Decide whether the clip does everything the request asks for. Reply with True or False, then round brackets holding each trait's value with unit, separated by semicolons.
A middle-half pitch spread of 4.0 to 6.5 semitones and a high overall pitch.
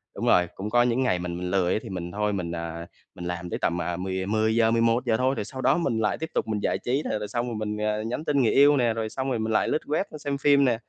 False (5.1 semitones; 110 Hz)